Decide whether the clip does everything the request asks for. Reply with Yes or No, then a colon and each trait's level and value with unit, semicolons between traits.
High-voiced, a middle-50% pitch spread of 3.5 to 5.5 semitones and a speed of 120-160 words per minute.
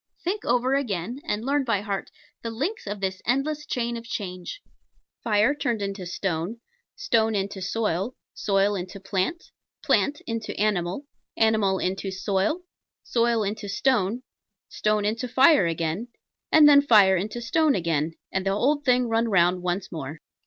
Yes: high, 215 Hz; average, 4.5 semitones; average, 150 wpm